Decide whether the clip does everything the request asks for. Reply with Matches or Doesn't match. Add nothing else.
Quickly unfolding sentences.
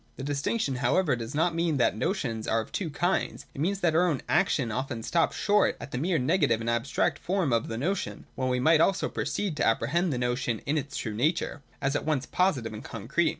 Matches